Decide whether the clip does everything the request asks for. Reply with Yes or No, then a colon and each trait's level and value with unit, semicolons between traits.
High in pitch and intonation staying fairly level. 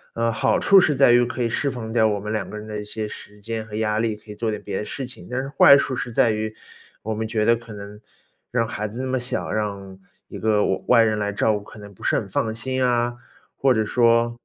No: low, 110 Hz; narrow, 2.3 semitones